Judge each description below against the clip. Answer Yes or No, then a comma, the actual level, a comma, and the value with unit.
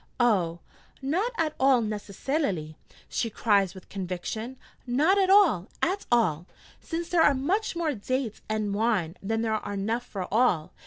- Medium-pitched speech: No, high, 225 Hz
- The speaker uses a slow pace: No, average, 150 wpm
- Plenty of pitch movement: Yes, wide, 6.6 semitones